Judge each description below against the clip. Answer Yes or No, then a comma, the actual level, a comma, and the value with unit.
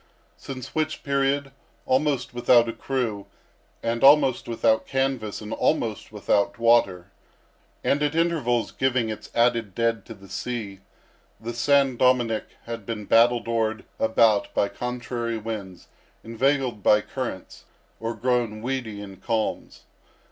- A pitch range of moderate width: Yes, average, 3.0 semitones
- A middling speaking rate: No, slow, 130 wpm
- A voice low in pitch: Yes, low, 115 Hz